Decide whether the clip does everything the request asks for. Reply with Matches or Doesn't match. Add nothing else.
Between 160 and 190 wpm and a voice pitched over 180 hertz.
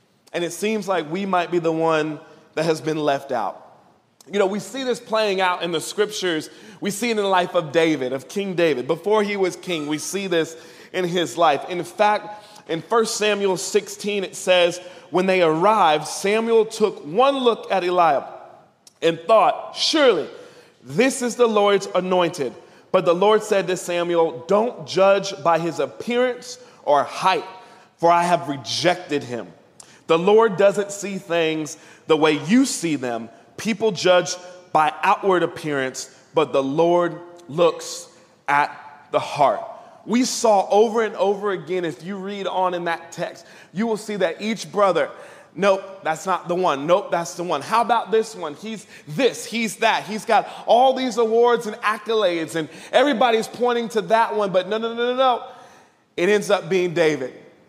Matches